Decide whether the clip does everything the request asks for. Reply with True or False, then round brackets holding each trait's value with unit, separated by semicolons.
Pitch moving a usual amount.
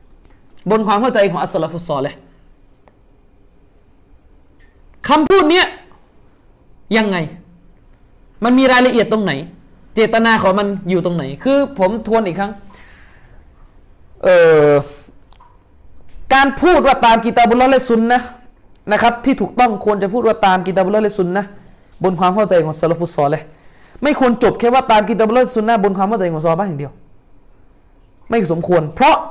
False (5.8 semitones)